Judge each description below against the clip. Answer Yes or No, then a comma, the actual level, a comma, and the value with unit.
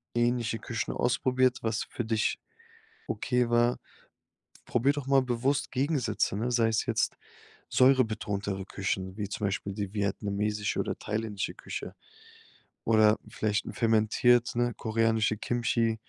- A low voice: Yes, low, 115 Hz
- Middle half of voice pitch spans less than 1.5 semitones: No, narrow, 2.4 semitones